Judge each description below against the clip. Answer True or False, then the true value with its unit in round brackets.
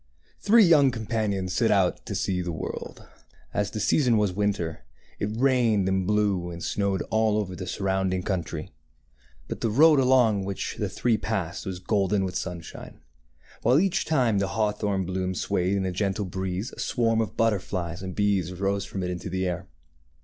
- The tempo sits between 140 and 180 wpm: False (190 wpm)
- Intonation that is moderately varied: True (3.1 semitones)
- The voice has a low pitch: True (100 Hz)